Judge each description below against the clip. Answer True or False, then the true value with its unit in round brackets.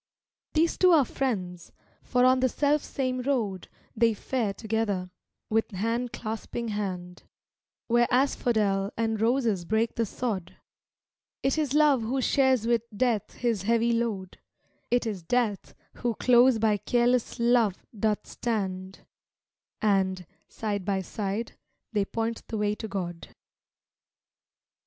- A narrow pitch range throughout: False (3.5 semitones)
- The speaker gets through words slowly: True (130 wpm)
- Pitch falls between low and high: False (225 Hz)